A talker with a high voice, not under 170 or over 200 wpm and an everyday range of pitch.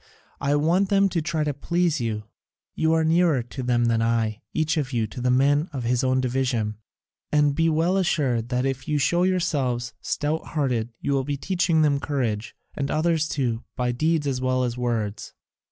No: medium, 140 Hz; average, 195 wpm; average, 4.5 semitones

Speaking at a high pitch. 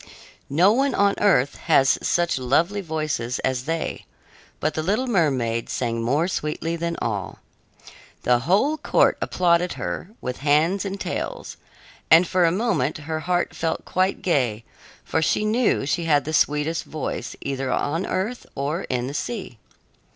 No: medium, 160 Hz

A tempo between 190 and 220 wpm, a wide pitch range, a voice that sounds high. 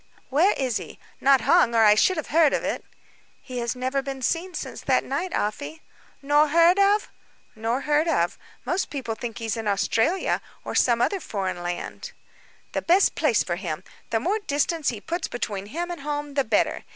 Yes: average, 195 wpm; wide, 6.6 semitones; very high, 275 Hz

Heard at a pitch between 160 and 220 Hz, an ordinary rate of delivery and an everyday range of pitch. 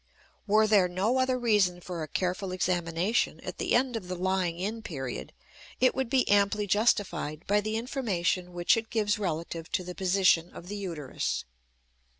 Yes: high, 190 Hz; average, 170 wpm; average, 3.6 semitones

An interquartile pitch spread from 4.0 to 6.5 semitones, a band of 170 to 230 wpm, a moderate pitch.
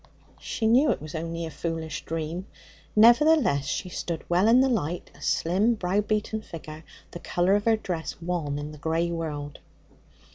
Yes: average, 4.9 semitones; average, 180 wpm; medium, 175 Hz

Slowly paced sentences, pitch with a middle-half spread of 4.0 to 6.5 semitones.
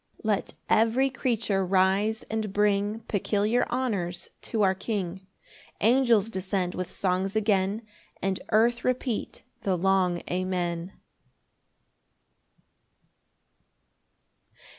No: slow, 95 wpm; average, 2.9 semitones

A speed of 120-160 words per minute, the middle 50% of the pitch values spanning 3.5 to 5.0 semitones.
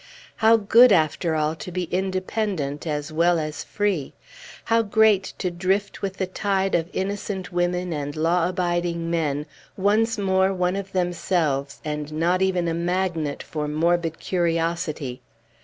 No: average, 145 wpm; average, 3.1 semitones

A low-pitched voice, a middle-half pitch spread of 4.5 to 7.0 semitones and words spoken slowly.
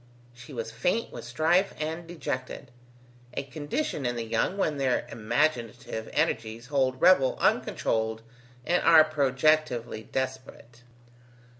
Yes: low, 130 Hz; average, 4.8 semitones; slow, 120 wpm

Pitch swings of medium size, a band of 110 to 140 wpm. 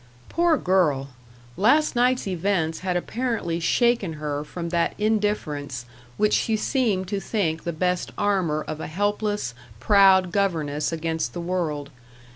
Yes: average, 4.6 semitones; slow, 135 wpm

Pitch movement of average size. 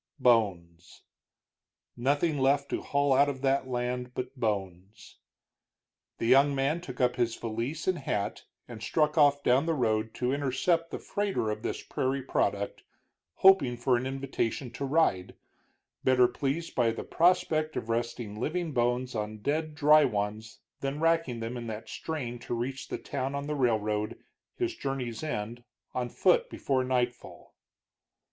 Yes: average, 3.9 semitones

